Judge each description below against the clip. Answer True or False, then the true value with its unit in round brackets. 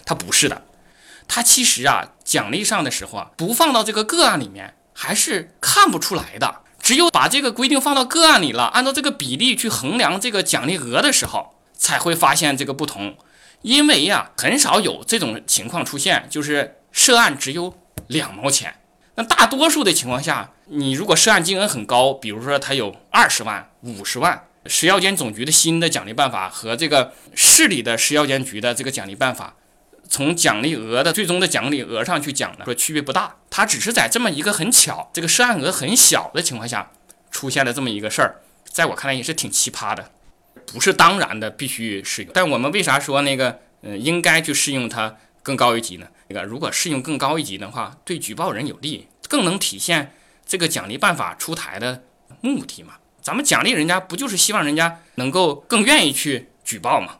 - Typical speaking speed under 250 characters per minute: False (305 characters per minute)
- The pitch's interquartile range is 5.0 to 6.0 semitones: False (9.0 semitones)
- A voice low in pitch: False (150 Hz)